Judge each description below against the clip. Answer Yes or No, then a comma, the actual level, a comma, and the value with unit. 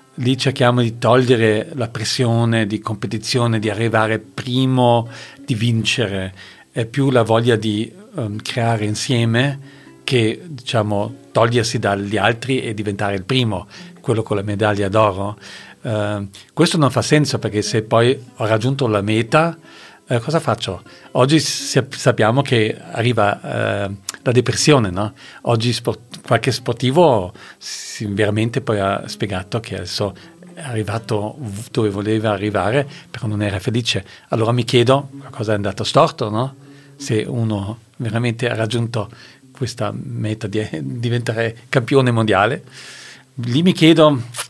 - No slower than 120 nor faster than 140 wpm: Yes, average, 135 wpm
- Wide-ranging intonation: No, average, 3.5 semitones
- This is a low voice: Yes, low, 115 Hz